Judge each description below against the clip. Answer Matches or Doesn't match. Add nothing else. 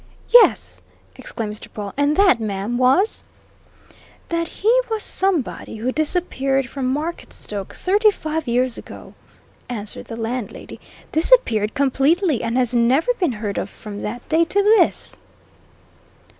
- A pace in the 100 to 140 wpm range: Matches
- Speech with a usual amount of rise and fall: Doesn't match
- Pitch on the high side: Matches